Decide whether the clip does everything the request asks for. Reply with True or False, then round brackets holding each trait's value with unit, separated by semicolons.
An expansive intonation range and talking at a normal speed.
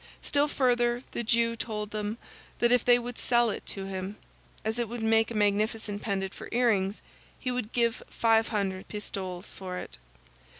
False (2.8 semitones; 175 wpm)